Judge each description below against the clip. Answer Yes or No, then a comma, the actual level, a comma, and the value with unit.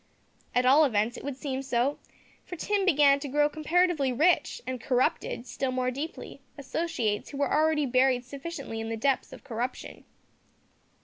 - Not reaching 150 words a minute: No, average, 165 wpm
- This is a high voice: Yes, very high, 275 Hz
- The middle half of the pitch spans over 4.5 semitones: No, average, 3.1 semitones